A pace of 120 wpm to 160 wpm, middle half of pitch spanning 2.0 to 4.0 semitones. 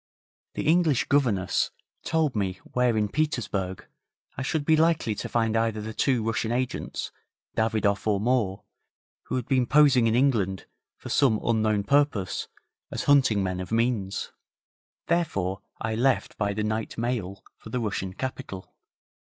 No: average, 150 wpm; average, 4.4 semitones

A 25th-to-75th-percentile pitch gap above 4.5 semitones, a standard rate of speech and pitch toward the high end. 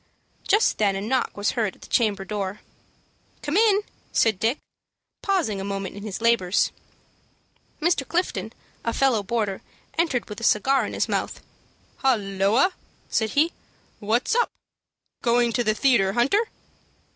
Yes: average, 5.1 semitones; average, 145 wpm; high, 230 Hz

